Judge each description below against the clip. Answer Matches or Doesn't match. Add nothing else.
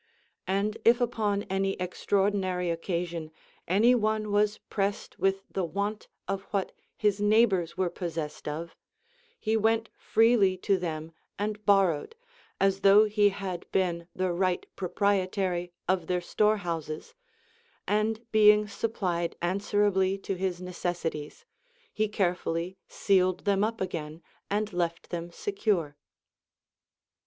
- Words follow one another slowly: Matches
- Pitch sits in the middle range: Doesn't match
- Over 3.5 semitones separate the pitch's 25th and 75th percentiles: Doesn't match